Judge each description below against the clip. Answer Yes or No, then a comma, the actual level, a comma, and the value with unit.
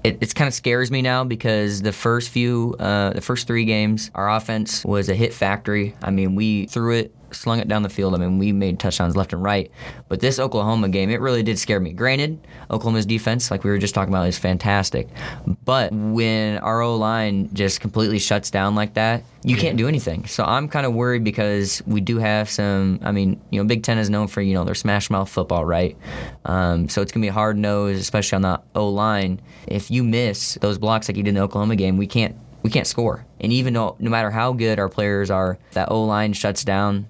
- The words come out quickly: Yes, fast, 235 wpm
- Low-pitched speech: Yes, low, 105 Hz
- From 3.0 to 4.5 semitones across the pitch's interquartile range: No, narrow, 2.6 semitones